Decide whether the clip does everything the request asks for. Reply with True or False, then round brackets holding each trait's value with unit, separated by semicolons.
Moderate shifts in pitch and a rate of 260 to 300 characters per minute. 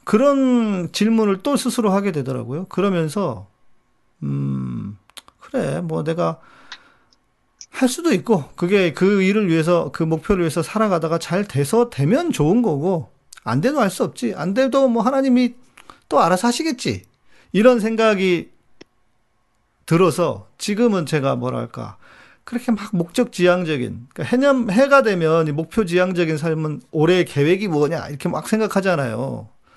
False (6.5 semitones; 290 characters per minute)